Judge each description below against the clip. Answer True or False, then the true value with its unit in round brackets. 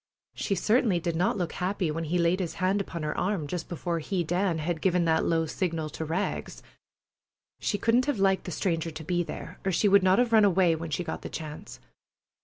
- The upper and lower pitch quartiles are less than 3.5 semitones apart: True (3.0 semitones)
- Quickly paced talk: True (225 wpm)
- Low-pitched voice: False (175 Hz)